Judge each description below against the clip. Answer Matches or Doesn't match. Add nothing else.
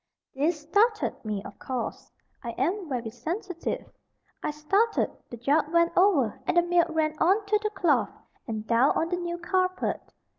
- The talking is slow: Doesn't match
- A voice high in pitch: Matches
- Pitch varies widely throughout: Matches